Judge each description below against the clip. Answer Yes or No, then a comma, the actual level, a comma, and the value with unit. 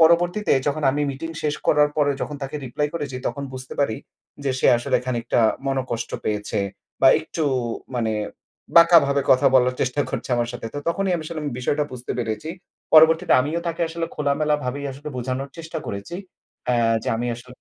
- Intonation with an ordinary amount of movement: Yes, average, 3.9 semitones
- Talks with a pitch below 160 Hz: Yes, medium, 140 Hz